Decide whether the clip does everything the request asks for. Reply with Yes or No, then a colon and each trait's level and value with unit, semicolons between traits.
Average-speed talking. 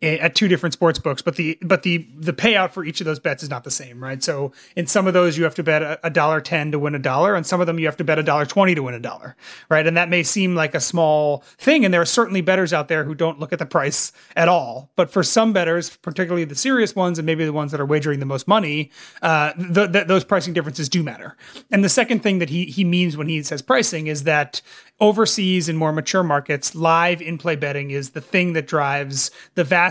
No: fast, 260 wpm